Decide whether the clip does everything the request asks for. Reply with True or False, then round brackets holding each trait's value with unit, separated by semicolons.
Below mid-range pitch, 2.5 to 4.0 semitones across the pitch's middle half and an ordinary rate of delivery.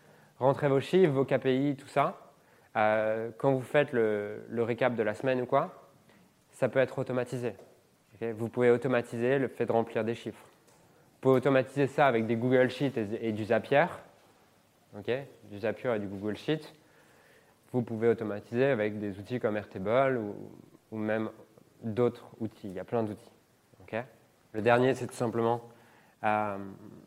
True (120 Hz; 3.1 semitones; 170 wpm)